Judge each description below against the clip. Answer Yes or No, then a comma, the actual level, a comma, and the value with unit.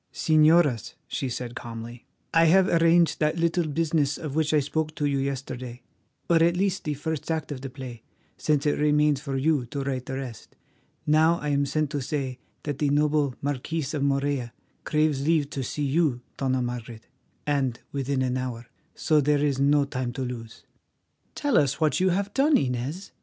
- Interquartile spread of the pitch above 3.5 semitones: No, average, 3.2 semitones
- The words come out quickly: No, average, 185 wpm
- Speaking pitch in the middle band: Yes, medium, 145 Hz